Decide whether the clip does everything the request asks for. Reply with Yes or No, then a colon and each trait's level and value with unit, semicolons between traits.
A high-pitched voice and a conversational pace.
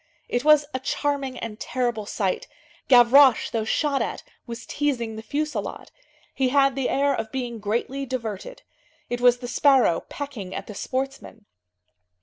Yes: very high, 250 Hz; average, 150 wpm